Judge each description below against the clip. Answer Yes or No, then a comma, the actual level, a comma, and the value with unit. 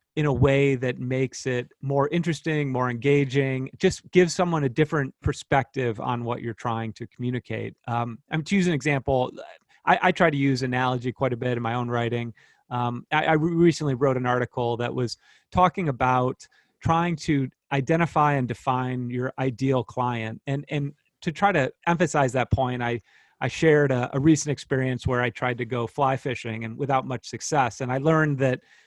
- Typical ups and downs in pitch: Yes, average, 3.0 semitones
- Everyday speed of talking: Yes, average, 185 wpm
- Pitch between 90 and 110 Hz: No, low, 130 Hz